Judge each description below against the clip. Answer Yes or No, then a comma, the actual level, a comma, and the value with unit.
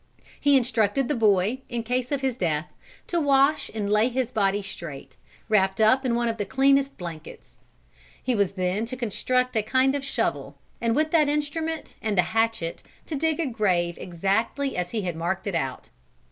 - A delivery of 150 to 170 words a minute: No, average, 190 wpm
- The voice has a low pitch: No, high, 225 Hz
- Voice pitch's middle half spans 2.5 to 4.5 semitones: No, wide, 5.5 semitones